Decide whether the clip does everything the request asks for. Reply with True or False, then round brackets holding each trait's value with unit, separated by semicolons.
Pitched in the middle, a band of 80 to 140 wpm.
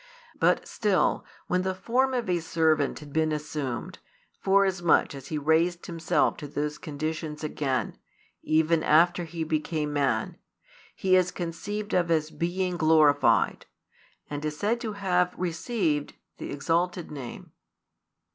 True (165 Hz; 135 wpm)